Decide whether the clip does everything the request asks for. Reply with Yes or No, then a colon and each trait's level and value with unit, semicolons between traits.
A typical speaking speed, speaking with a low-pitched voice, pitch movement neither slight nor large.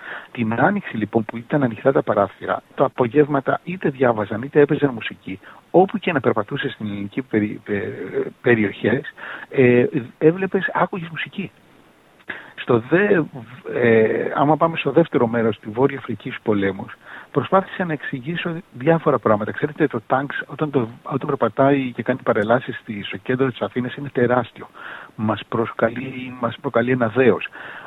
Yes: average, 145 wpm; low, 130 Hz; average, 4.4 semitones